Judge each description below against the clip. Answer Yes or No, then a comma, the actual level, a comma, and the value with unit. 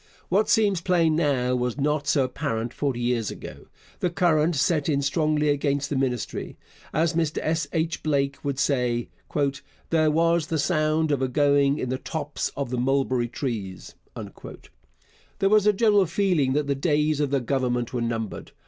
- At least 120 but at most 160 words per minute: No, average, 170 wpm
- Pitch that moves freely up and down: No, average, 3.6 semitones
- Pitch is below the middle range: No, medium, 145 Hz